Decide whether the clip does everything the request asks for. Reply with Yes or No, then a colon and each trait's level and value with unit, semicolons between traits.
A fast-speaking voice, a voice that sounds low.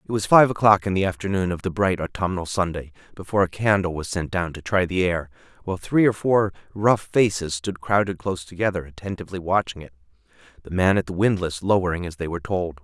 Yes: fast, 210 wpm; very low, 95 Hz